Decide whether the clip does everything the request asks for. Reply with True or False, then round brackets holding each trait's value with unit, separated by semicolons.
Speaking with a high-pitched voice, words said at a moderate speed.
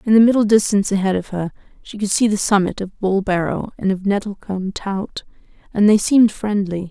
True (200 Hz; 190 wpm)